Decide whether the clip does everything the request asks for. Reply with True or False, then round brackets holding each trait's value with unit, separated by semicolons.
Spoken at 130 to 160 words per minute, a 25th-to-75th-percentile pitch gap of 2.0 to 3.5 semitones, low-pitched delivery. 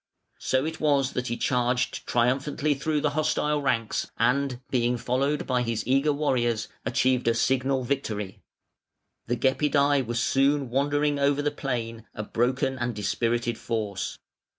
True (145 wpm; 3.0 semitones; 130 Hz)